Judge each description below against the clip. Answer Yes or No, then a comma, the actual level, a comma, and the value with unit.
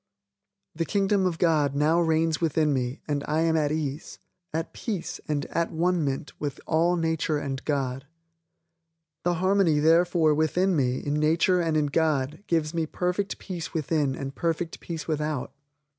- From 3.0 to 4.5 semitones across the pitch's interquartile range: No, narrow, 2.4 semitones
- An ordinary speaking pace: Yes, average, 160 wpm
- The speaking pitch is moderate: Yes, medium, 160 Hz